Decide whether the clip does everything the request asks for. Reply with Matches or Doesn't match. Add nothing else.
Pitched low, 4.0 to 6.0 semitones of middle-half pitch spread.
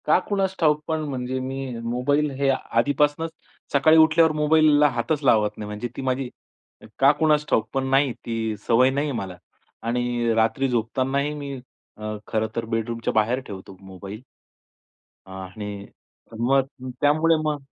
Matches